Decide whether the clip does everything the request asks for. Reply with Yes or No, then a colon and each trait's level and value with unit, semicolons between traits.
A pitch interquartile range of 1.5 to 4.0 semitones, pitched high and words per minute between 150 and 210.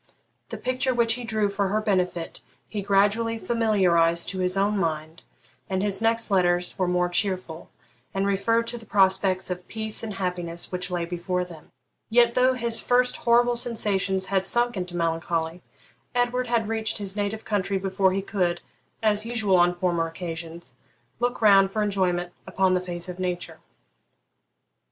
Yes: average, 3.7 semitones; high, 195 Hz; average, 165 wpm